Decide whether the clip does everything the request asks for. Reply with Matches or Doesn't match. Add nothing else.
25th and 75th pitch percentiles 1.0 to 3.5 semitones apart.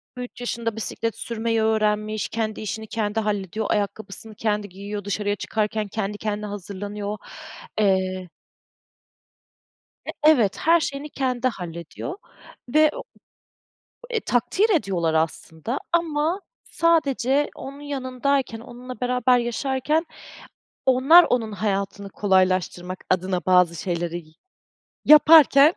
Doesn't match